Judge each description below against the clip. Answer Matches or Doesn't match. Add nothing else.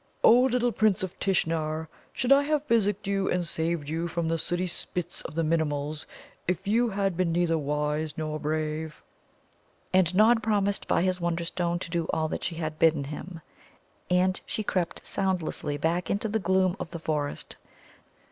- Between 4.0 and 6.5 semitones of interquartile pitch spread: Doesn't match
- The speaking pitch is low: Doesn't match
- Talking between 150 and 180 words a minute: Matches